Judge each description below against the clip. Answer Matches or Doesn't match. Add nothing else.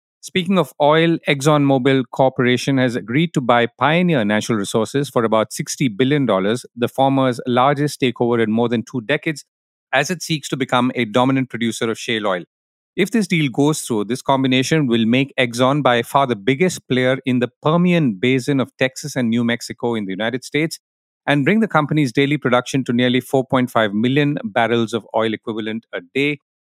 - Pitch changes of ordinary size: Matches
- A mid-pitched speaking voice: Doesn't match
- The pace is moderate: Matches